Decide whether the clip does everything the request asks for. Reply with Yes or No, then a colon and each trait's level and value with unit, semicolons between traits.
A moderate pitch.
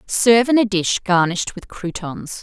No: high, 200 Hz